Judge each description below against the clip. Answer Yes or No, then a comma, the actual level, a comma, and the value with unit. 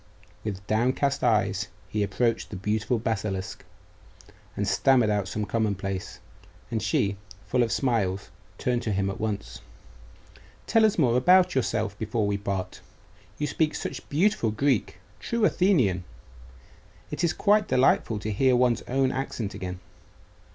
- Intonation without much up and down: No, average, 4.7 semitones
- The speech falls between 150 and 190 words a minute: No, average, 140 wpm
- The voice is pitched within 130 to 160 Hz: No, low, 110 Hz